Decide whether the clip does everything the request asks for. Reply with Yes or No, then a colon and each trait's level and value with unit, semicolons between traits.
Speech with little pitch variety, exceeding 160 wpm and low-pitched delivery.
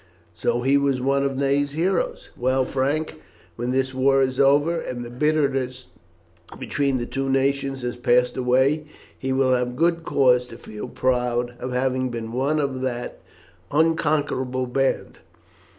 No: narrow, 1.9 semitones; average, 150 wpm; low, 130 Hz